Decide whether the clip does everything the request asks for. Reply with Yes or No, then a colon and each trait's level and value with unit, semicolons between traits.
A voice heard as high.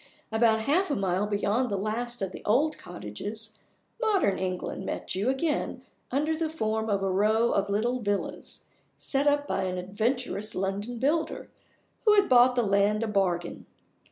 Yes: high, 220 Hz